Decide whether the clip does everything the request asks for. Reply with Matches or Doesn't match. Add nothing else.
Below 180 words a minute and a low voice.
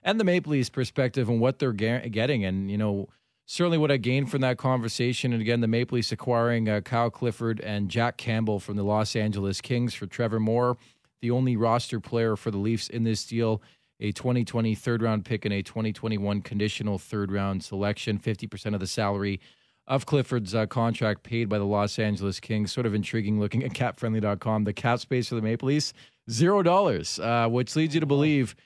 Doesn't match